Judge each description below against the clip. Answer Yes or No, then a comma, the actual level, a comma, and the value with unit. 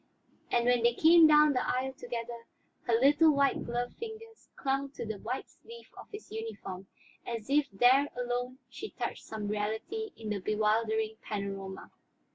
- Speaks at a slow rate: No, average, 160 wpm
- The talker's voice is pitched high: Yes, high, 245 Hz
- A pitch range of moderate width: Yes, average, 4.5 semitones